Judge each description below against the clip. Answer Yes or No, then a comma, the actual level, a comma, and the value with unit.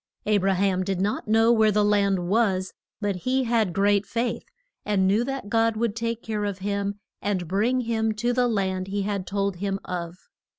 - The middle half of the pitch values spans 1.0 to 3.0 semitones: Yes, narrow, 2.6 semitones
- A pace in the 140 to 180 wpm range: No, average, 200 wpm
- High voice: Yes, high, 205 Hz